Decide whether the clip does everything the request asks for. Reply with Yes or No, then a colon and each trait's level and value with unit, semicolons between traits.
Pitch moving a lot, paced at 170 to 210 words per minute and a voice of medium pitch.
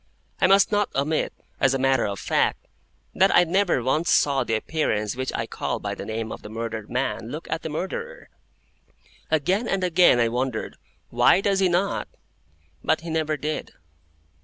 Yes: wide, 6.9 semitones; average, 180 wpm; medium, 155 Hz